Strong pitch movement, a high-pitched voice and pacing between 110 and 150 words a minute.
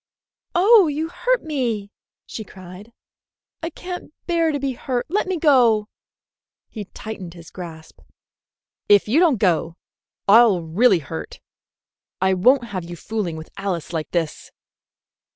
Yes: wide, 8.3 semitones; high, 215 Hz; slow, 135 wpm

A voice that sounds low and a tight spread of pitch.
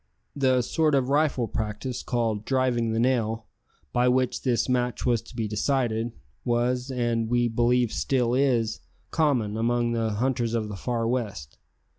Yes: low, 120 Hz; narrow, 2.1 semitones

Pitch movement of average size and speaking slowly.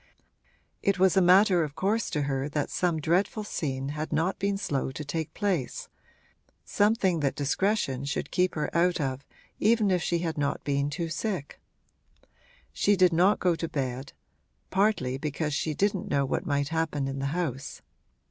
No: average, 4.9 semitones; average, 170 wpm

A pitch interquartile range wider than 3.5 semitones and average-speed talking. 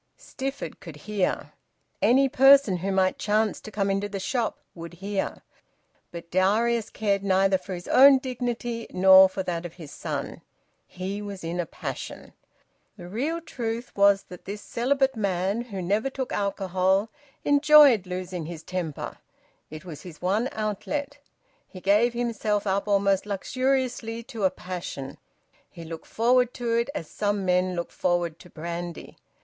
Yes: average, 4.5 semitones; average, 155 wpm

